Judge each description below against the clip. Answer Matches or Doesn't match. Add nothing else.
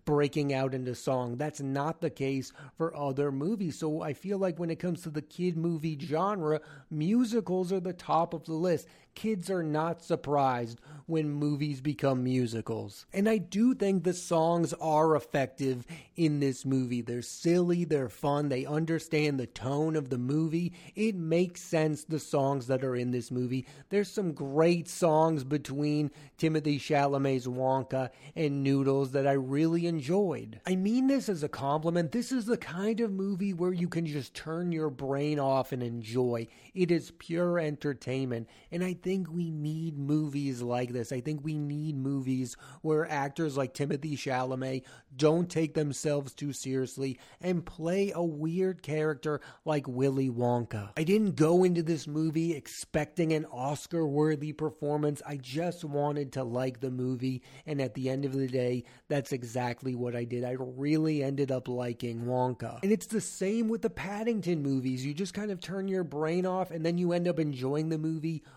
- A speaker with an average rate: Matches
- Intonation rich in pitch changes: Doesn't match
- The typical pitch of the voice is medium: Matches